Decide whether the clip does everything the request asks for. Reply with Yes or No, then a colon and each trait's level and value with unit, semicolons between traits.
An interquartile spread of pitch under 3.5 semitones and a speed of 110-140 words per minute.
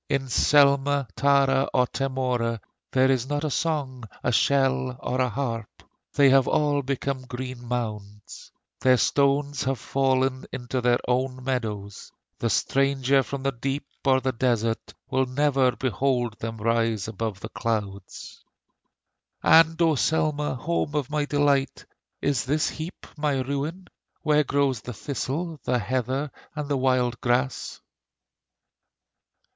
Yes: narrow, 2.4 semitones; slow, 135 wpm